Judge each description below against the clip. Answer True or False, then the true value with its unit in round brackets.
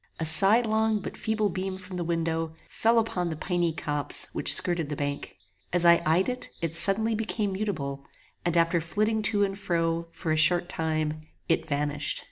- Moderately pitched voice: True (175 Hz)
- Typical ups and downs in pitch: True (4.1 semitones)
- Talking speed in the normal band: True (180 wpm)